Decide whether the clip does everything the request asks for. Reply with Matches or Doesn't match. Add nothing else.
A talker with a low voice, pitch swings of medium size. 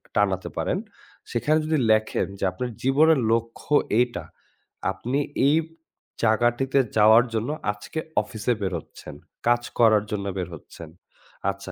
Matches